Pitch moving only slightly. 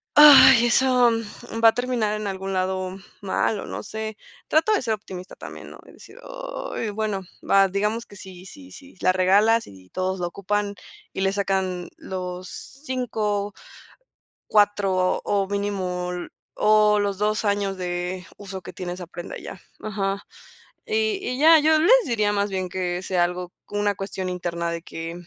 No: average, 3.3 semitones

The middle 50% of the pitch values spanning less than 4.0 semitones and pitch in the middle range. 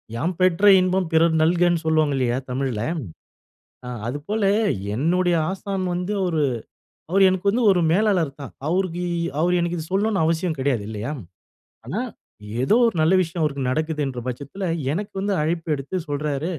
No: average, 4.3 semitones; medium, 165 Hz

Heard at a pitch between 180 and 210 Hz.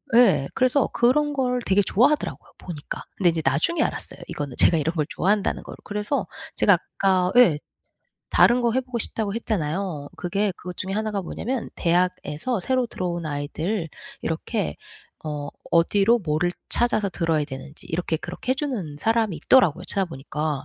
Yes: medium, 185 Hz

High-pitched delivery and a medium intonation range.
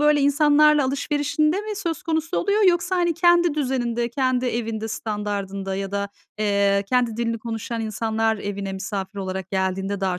No: high, 230 Hz; wide, 6.9 semitones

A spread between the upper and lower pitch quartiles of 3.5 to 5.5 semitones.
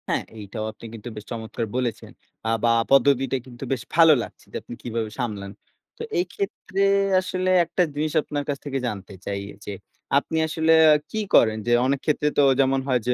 Yes: average, 5.1 semitones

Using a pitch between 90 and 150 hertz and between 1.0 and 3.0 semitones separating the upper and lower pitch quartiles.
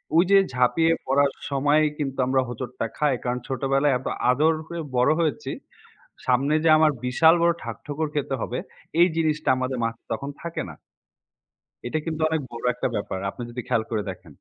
No: low, 135 Hz; average, 3.9 semitones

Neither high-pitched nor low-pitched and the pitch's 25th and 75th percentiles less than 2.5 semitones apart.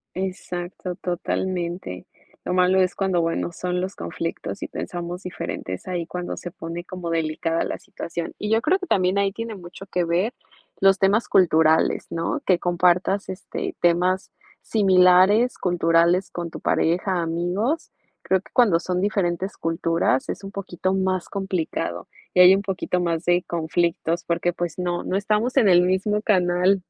Yes: medium, 180 Hz; narrow, 2.0 semitones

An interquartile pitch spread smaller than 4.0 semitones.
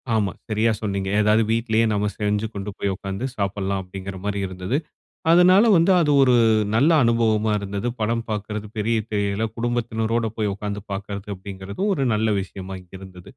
Yes: narrow, 2.6 semitones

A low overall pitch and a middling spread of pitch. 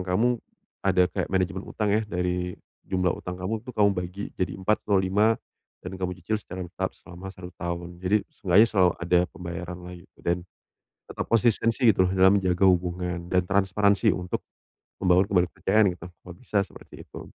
No: very low, 90 Hz; narrow, 2.0 semitones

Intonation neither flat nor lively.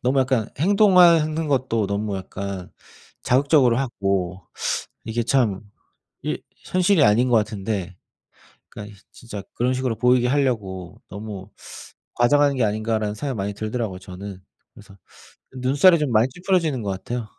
Yes: average, 4.9 semitones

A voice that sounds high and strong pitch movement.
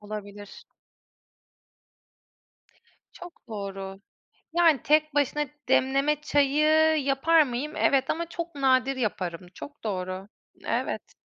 Yes: very high, 270 Hz; wide, 6.6 semitones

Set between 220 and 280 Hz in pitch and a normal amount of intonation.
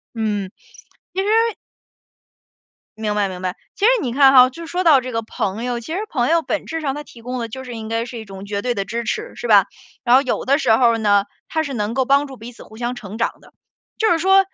Yes: high, 245 Hz; average, 4.3 semitones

